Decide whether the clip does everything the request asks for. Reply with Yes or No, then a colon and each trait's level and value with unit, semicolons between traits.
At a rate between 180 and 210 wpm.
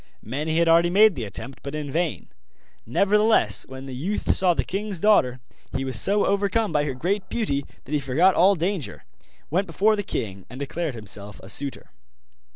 Yes: average, 185 wpm